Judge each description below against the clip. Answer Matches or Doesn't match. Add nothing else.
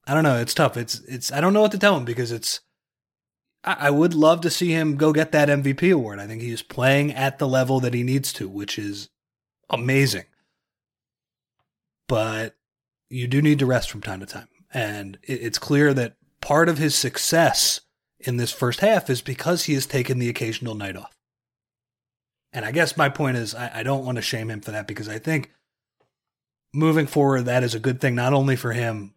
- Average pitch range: Matches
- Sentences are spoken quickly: Matches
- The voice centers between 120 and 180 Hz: Matches